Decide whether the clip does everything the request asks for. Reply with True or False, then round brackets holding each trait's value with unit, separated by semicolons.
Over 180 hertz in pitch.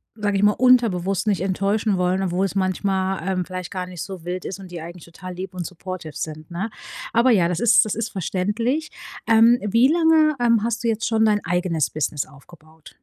True (190 Hz)